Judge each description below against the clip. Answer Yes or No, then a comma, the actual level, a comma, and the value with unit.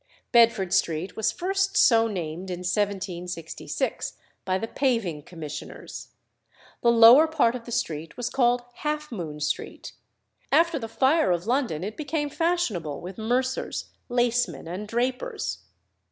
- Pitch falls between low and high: No, high, 225 Hz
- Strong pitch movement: Yes, wide, 6.5 semitones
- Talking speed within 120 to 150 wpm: Yes, slow, 135 wpm